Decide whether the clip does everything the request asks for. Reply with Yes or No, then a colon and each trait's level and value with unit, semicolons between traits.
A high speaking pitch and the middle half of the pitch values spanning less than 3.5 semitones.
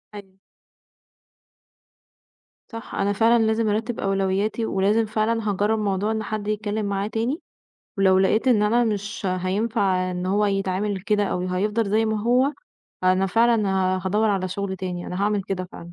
Yes: high, 205 Hz; narrow, 2.4 semitones